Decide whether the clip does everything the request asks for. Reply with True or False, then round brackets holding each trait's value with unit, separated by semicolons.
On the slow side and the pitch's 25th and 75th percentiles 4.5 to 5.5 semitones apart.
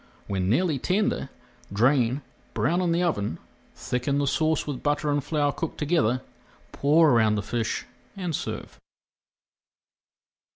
True (130 wpm; 5.1 semitones)